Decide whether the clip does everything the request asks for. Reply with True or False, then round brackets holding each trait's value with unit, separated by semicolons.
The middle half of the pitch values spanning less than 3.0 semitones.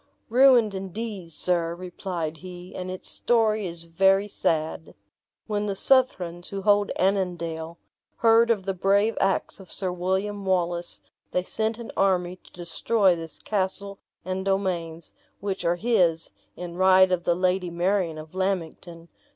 True (2.6 semitones)